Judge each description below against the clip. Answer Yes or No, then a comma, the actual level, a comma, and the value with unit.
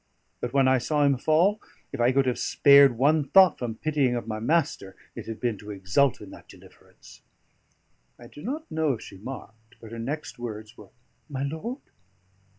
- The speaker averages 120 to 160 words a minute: No, average, 190 wpm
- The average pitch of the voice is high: No, low, 130 Hz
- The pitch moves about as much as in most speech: Yes, average, 4.9 semitones